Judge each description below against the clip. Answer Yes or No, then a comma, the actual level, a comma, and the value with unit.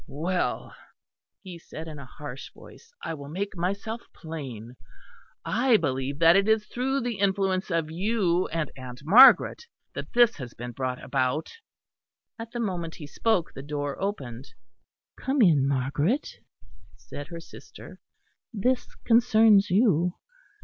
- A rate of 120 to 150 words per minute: Yes, average, 140 wpm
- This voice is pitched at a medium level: Yes, medium, 170 Hz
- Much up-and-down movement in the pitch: Yes, wide, 7.1 semitones